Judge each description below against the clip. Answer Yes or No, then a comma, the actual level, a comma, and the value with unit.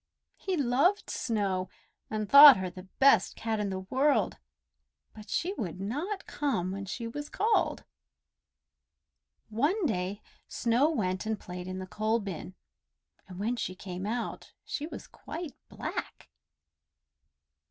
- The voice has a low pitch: No, high, 220 Hz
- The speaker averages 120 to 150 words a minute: Yes, slow, 135 wpm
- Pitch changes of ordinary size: No, wide, 7.1 semitones